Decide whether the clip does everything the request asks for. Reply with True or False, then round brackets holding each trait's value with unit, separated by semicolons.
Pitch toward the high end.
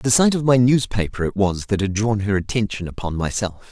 False (105 Hz)